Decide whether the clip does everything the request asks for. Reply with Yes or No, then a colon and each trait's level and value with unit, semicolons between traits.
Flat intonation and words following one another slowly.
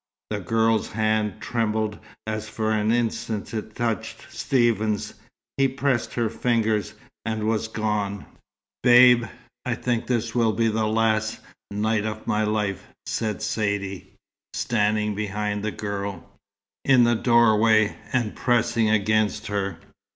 Yes: narrow, 1.4 semitones; slow, 130 wpm